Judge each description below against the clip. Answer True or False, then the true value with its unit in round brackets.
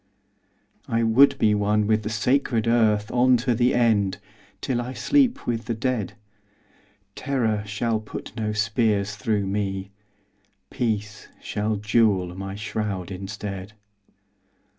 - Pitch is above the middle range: False (110 Hz)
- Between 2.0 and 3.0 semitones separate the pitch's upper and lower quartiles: True (2.6 semitones)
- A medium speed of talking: False (125 wpm)